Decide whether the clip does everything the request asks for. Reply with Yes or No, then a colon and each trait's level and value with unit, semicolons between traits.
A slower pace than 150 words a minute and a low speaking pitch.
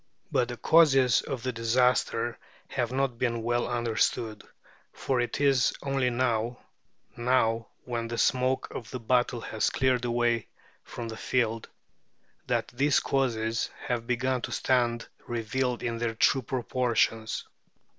Yes: slow, 135 wpm; low, 120 Hz